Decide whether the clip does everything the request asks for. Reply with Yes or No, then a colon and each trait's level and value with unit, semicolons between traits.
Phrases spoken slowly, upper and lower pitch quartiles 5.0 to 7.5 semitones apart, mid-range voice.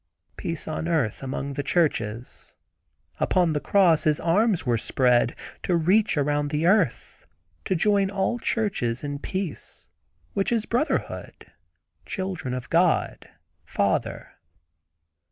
Yes: slow, 120 wpm; wide, 5.4 semitones; medium, 165 Hz